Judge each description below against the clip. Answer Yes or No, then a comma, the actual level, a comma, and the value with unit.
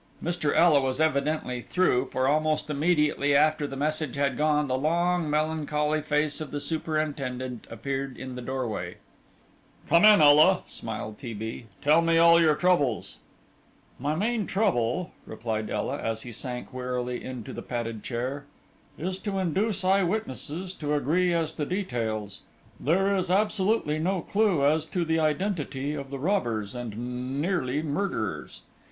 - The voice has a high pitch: No, medium, 150 Hz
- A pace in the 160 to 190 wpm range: No, average, 150 wpm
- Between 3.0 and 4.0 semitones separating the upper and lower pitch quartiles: No, average, 4.8 semitones